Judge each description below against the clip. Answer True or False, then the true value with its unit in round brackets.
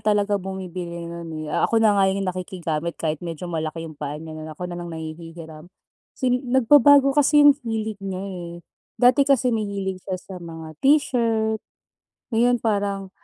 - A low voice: False (190 Hz)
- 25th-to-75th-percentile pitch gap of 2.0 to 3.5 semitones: False (5.0 semitones)